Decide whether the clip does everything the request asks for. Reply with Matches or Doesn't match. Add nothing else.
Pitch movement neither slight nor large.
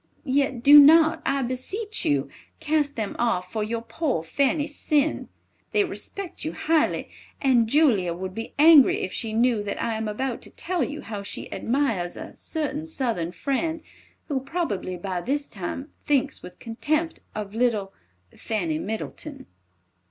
Doesn't match